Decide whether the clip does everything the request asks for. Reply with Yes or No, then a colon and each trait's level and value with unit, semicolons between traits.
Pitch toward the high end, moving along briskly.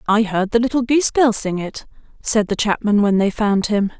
Yes: high, 215 Hz; fast, 225 wpm